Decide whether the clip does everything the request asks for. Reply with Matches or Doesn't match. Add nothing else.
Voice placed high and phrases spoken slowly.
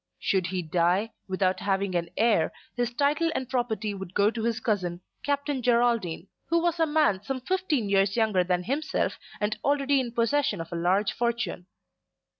Doesn't match